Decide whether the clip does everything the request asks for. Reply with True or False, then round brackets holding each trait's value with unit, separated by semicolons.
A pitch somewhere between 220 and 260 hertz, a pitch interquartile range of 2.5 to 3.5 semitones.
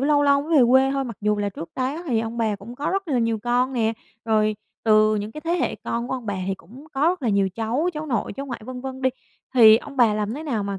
False (240 Hz; 4.3 semitones)